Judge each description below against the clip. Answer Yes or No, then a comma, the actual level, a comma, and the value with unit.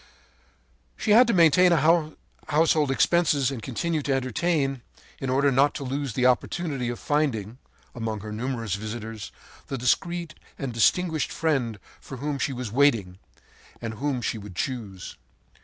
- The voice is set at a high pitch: No, low, 135 Hz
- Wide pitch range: No, average, 4.8 semitones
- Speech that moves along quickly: No, average, 150 wpm